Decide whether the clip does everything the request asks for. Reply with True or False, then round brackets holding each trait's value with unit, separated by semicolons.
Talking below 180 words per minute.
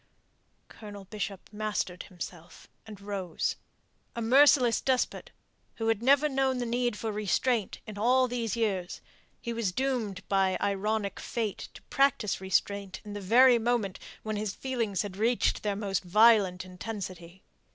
True (145 wpm)